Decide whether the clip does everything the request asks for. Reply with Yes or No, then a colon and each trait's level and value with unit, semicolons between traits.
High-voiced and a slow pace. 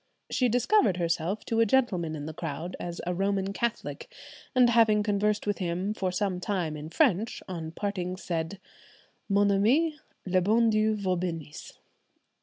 No: high, 195 Hz; average, 160 wpm